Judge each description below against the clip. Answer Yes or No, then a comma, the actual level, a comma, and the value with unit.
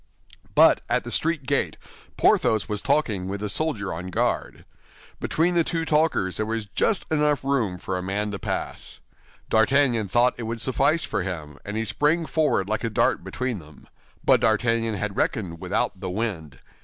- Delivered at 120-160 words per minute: No, average, 180 wpm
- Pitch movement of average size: No, wide, 6.3 semitones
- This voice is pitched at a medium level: No, low, 110 Hz